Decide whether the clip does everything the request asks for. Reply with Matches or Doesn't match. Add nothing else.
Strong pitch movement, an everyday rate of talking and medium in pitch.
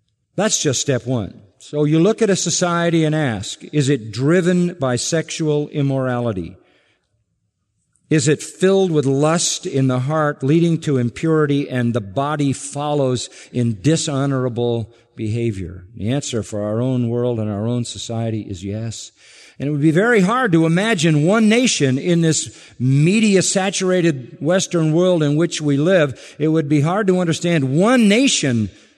Matches